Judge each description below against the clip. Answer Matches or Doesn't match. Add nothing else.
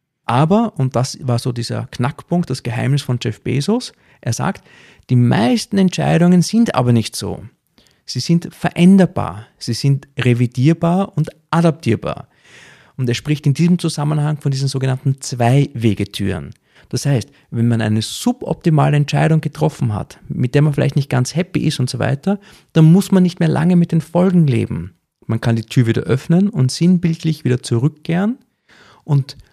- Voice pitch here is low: Doesn't match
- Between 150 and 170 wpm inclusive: Matches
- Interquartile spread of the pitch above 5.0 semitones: Matches